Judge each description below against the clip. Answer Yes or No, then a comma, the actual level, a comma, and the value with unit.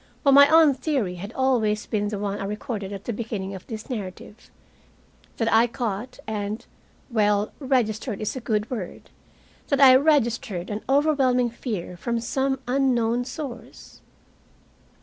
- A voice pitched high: Yes, high, 230 Hz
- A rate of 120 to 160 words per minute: Yes, average, 150 wpm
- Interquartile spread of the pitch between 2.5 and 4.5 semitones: Yes, average, 4.0 semitones